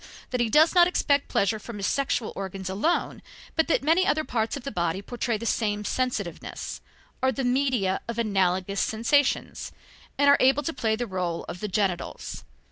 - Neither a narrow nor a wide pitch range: No, wide, 5.9 semitones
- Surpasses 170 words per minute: Yes, average, 185 wpm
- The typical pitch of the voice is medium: No, high, 230 Hz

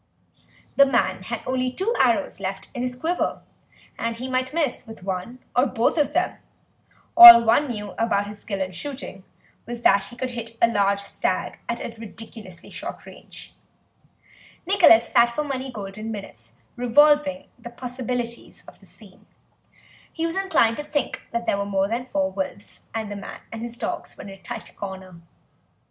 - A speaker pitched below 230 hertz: No, high, 235 Hz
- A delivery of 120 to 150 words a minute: No, average, 180 wpm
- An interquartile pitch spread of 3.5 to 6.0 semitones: Yes, average, 4.2 semitones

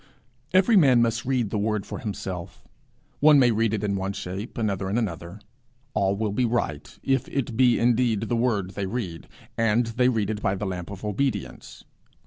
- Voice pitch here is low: Yes, low, 110 Hz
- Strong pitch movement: No, average, 3.6 semitones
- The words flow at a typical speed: Yes, average, 190 wpm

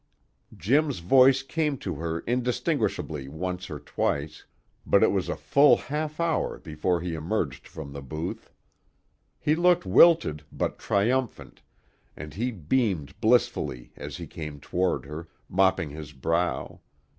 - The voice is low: Yes, very low, 90 Hz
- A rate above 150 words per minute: No, slow, 135 wpm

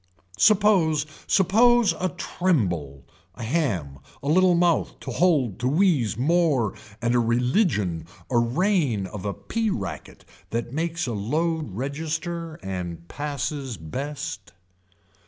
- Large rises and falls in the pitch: Yes, wide, 8.3 semitones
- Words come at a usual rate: No, slow, 120 wpm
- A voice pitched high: No, medium, 140 Hz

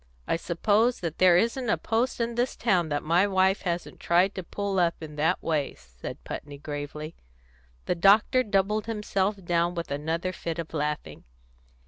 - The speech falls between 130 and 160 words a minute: No, average, 170 wpm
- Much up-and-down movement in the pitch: No, average, 4.2 semitones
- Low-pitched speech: No, medium, 175 Hz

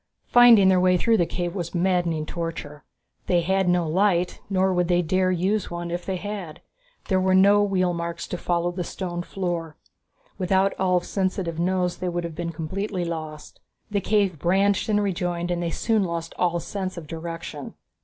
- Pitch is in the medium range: Yes, medium, 180 Hz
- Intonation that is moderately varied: No, narrow, 2.0 semitones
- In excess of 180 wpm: Yes, average, 190 wpm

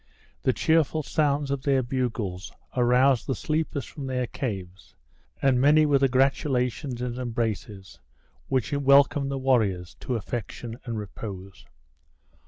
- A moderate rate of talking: No, slow, 130 wpm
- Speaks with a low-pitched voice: Yes, low, 130 Hz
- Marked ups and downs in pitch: No, average, 3.5 semitones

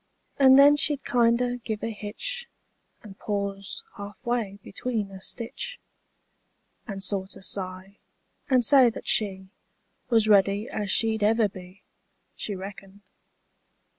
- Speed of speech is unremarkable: No, slow, 125 wpm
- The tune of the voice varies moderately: Yes, average, 3.5 semitones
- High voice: Yes, high, 210 Hz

